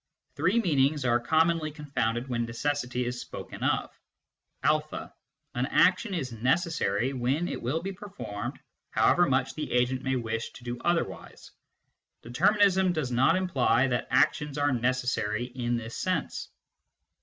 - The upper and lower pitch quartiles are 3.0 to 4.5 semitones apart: No, average, 5.2 semitones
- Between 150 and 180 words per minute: No, average, 140 wpm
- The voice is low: Yes, low, 130 Hz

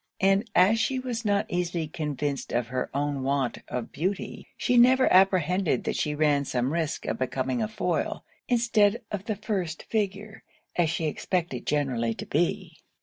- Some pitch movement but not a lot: No, wide, 6.7 semitones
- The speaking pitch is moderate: Yes, medium, 175 Hz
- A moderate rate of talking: Yes, average, 165 wpm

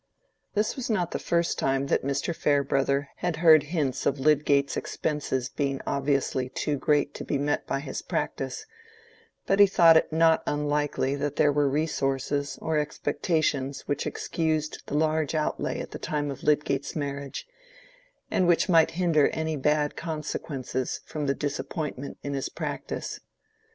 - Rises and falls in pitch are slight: Yes, narrow, 2.3 semitones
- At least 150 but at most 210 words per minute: Yes, average, 155 wpm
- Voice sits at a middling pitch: Yes, medium, 145 Hz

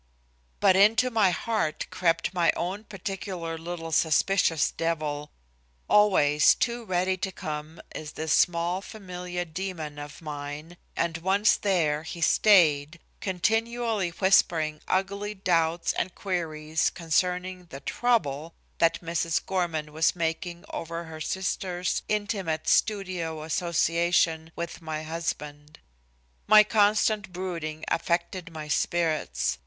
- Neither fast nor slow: No, slow, 115 wpm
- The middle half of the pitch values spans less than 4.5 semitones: Yes, average, 3.1 semitones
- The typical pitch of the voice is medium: Yes, medium, 170 Hz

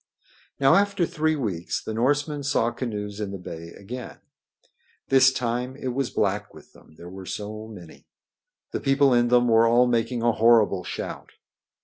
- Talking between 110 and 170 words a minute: Yes, average, 165 wpm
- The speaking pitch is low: Yes, low, 120 Hz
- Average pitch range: Yes, average, 4.1 semitones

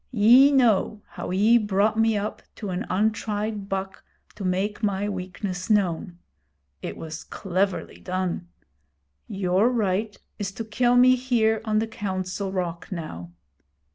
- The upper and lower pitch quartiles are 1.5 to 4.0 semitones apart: Yes, average, 2.9 semitones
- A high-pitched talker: Yes, high, 205 Hz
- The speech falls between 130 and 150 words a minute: Yes, average, 140 wpm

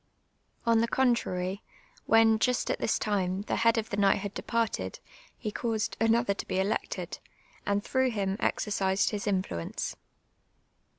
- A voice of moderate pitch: No, high, 210 Hz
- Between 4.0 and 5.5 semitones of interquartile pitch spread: No, average, 2.8 semitones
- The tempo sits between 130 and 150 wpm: Yes, average, 140 wpm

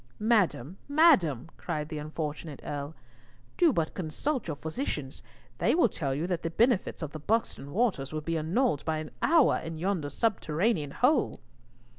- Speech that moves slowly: No, average, 165 wpm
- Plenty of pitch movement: Yes, wide, 7.2 semitones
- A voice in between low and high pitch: Yes, medium, 165 Hz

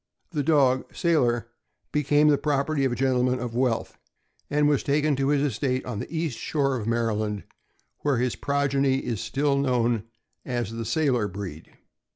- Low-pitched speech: Yes, low, 130 Hz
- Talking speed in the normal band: Yes, average, 165 wpm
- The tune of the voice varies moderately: Yes, average, 3.5 semitones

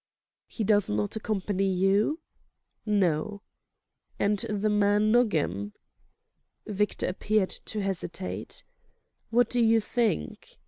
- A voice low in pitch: No, high, 205 Hz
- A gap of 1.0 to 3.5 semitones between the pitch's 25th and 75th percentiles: Yes, narrow, 2.4 semitones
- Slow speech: Yes, slow, 100 wpm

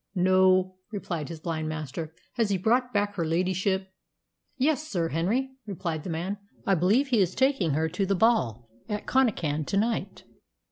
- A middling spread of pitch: Yes, average, 4.8 semitones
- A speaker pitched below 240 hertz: Yes, medium, 185 Hz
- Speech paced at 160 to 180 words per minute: Yes, average, 175 wpm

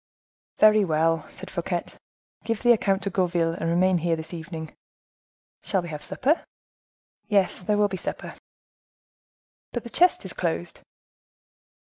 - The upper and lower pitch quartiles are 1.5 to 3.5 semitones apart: No, average, 3.9 semitones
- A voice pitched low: No, medium, 185 Hz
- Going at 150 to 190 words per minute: No, average, 140 wpm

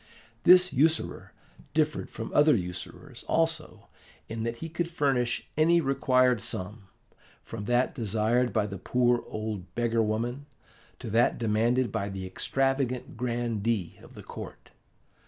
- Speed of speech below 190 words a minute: Yes, slow, 135 wpm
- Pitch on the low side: Yes, low, 120 Hz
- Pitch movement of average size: Yes, average, 4.0 semitones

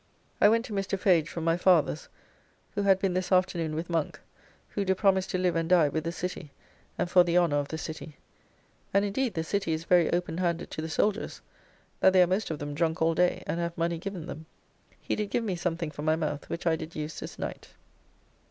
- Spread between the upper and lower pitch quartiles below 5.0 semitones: Yes, average, 2.7 semitones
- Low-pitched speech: No, medium, 170 Hz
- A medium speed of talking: No, fast, 230 wpm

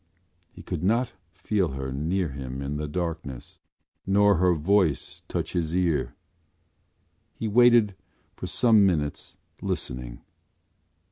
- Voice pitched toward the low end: Yes, very low, 85 Hz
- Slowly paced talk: Yes, slow, 120 wpm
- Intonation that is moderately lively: No, wide, 5.9 semitones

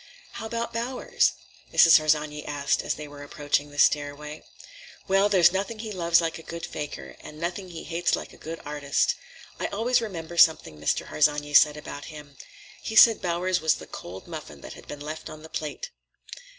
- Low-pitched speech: No, medium, 160 Hz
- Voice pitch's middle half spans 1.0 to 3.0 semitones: No, average, 4.1 semitones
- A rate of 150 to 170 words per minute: No, average, 190 wpm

